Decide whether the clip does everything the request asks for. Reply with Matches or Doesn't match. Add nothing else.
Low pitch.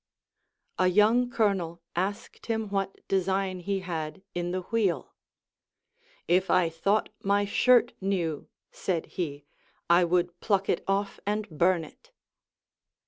Doesn't match